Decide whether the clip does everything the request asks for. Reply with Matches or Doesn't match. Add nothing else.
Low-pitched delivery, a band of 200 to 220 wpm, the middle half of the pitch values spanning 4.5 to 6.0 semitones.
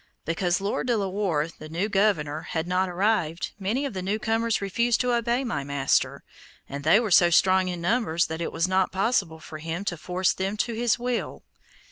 Doesn't match